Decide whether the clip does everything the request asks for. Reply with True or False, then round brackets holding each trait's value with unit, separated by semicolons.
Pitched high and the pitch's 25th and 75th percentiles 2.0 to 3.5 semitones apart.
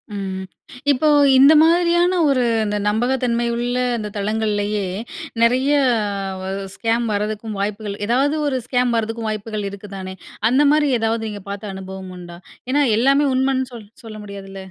False (225 Hz; 4.2 semitones)